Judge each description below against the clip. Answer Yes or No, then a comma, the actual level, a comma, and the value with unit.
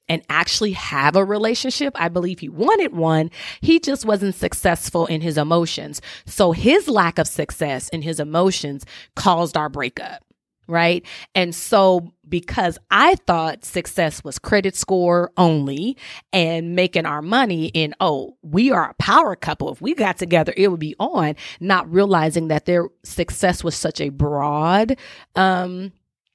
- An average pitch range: Yes, average, 3.3 semitones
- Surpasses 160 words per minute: No, average, 155 wpm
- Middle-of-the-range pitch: Yes, medium, 175 Hz